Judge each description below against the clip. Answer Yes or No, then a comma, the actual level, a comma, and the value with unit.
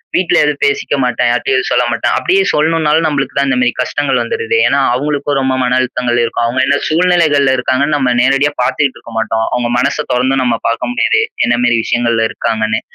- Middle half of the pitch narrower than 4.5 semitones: Yes, average, 3.3 semitones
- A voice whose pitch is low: Yes, low, 130 Hz